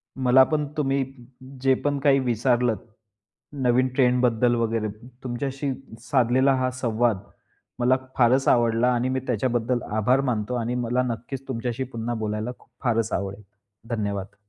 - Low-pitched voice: Yes, low, 125 Hz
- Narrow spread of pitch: Yes, narrow, 2.3 semitones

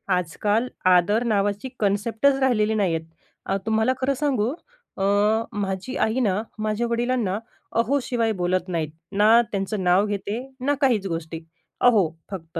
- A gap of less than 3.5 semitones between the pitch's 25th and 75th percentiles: No, average, 3.8 semitones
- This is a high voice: Yes, high, 210 Hz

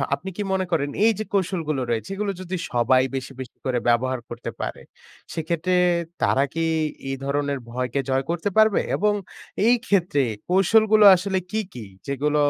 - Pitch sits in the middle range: Yes, medium, 160 Hz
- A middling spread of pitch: No, wide, 6.5 semitones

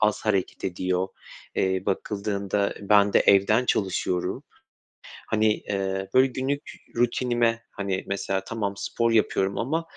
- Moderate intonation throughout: Yes, average, 3.1 semitones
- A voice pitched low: Yes, low, 100 Hz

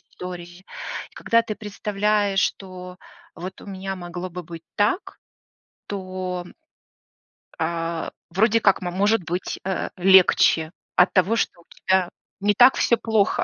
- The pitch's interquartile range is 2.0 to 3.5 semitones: Yes, narrow, 2.5 semitones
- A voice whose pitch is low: No, high, 190 Hz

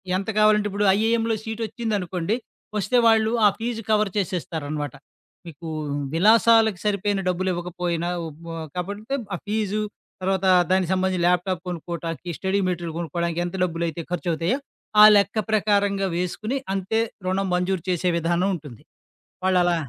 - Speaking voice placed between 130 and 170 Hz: No, medium, 185 Hz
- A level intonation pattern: No, average, 3.4 semitones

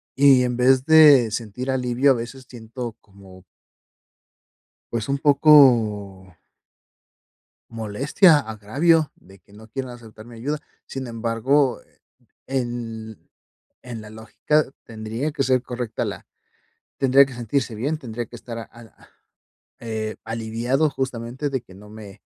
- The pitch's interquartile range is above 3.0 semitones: Yes, average, 3.4 semitones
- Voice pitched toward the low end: Yes, low, 120 Hz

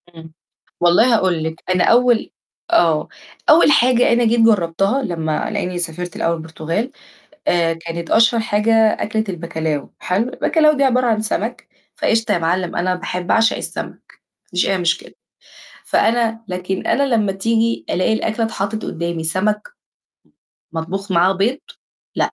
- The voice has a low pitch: No, high, 195 Hz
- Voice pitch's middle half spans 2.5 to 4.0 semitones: No, average, 4.9 semitones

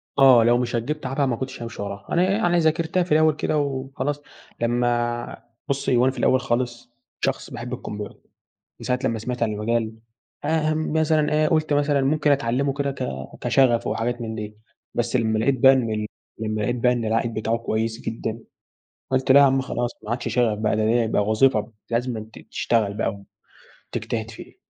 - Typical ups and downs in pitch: Yes, average, 3.6 semitones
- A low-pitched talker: Yes, low, 120 Hz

